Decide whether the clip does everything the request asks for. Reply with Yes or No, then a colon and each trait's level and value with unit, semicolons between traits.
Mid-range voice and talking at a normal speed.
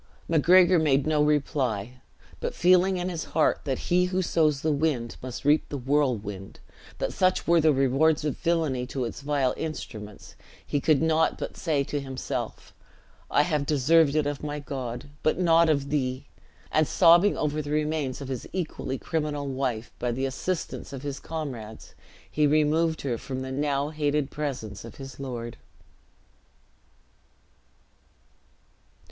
Yes: medium, 145 Hz; average, 155 wpm